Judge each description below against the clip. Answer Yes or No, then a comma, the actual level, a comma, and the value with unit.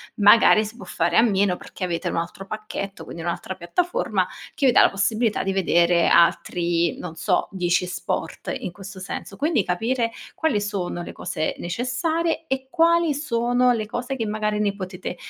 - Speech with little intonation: No, wide, 5.5 semitones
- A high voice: Yes, high, 205 Hz